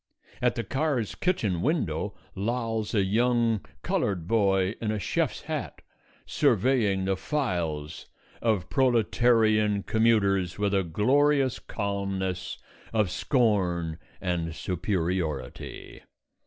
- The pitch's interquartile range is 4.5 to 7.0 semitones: No, average, 4.0 semitones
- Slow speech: Yes, slow, 100 wpm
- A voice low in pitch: Yes, low, 105 Hz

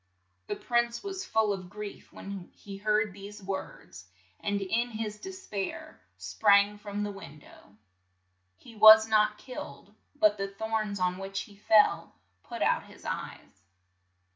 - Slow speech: No, average, 155 wpm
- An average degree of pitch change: No, narrow, 2.1 semitones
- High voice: Yes, high, 205 Hz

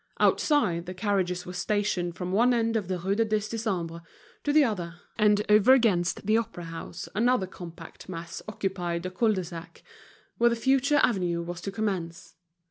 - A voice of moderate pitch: No, high, 195 Hz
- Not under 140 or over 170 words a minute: No, average, 180 wpm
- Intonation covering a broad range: No, average, 4.1 semitones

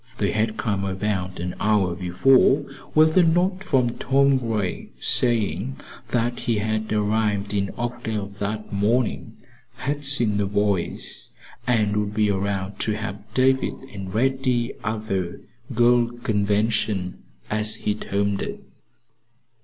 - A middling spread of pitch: Yes, average, 3.2 semitones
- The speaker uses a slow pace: Yes, slow, 130 wpm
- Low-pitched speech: Yes, low, 110 Hz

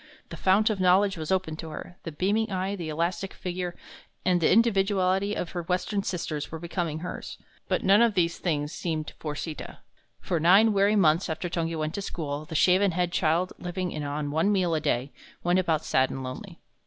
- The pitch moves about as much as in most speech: Yes, average, 3.3 semitones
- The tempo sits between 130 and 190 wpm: No, average, 200 wpm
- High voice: No, medium, 175 Hz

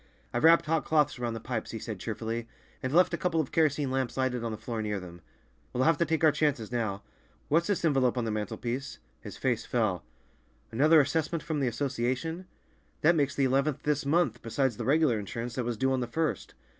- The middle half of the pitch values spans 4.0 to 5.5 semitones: Yes, average, 4.8 semitones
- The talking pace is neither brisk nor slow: No, fast, 215 wpm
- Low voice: Yes, low, 130 Hz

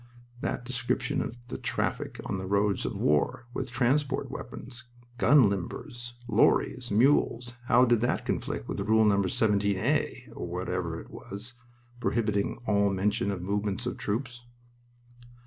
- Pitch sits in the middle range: No, low, 105 Hz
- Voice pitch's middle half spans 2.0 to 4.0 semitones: Yes, average, 3.5 semitones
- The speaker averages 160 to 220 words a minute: No, average, 140 wpm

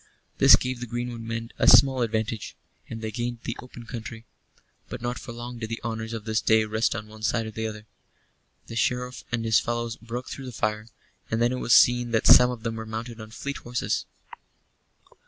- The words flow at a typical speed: No, fast, 210 wpm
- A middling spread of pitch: No, narrow, 1.5 semitones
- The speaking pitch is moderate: No, low, 115 Hz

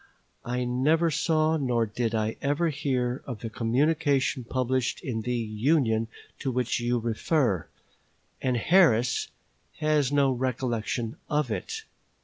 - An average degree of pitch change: Yes, average, 3.8 semitones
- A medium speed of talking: No, slow, 125 wpm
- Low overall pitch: Yes, low, 125 Hz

